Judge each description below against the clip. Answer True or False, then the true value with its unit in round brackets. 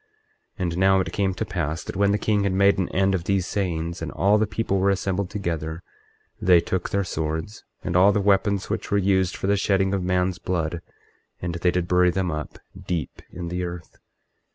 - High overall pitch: False (95 Hz)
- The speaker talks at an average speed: False (215 wpm)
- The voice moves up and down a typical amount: False (2.2 semitones)